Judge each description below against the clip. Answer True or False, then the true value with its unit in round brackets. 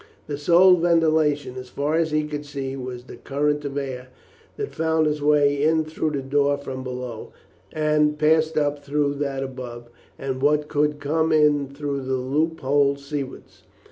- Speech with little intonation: True (2.0 semitones)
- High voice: False (145 Hz)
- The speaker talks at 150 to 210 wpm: True (170 wpm)